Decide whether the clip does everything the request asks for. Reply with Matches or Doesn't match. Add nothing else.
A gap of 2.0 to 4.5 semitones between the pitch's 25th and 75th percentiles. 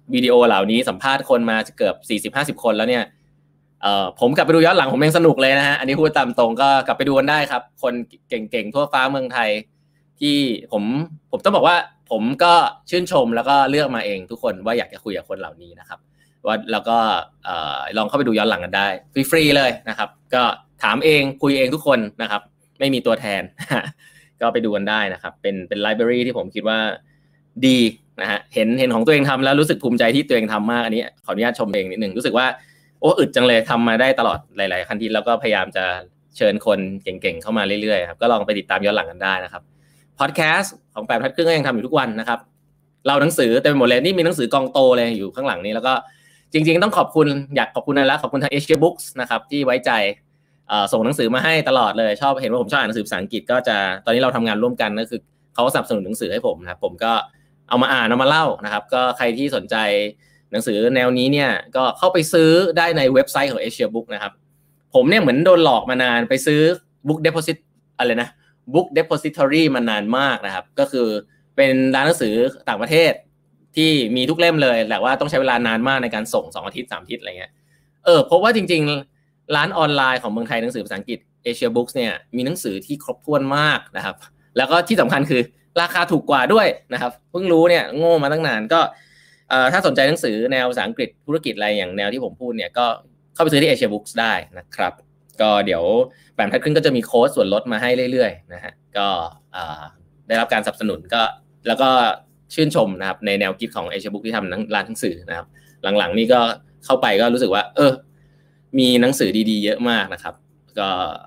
Doesn't match